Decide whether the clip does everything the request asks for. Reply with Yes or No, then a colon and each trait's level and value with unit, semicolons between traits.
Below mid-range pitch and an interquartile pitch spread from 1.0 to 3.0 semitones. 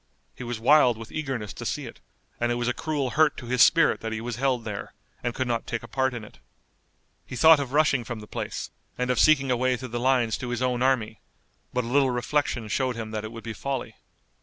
Yes: low, 125 Hz; narrow, 2.5 semitones